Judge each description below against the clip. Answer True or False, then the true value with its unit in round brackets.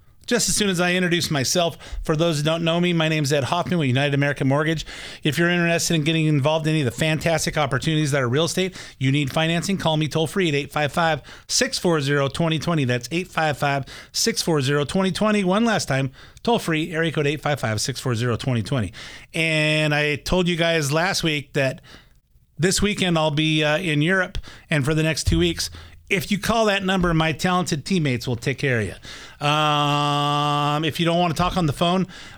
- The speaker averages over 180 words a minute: True (200 wpm)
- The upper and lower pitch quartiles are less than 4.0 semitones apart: True (3.3 semitones)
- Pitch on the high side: False (155 Hz)